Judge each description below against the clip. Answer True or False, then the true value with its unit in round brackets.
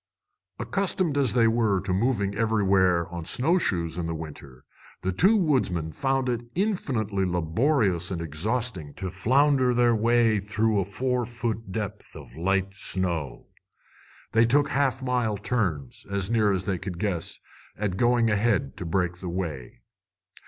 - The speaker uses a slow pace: False (150 wpm)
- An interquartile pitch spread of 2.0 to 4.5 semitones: False (5.4 semitones)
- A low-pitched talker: True (105 Hz)